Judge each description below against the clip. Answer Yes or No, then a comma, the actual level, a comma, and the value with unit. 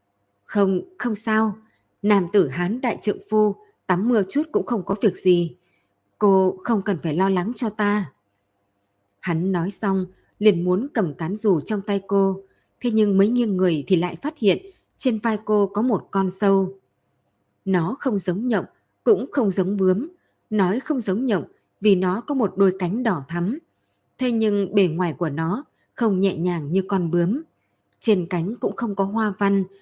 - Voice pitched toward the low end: No, high, 195 Hz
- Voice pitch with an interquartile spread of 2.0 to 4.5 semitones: Yes, average, 3.2 semitones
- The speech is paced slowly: No, average, 185 wpm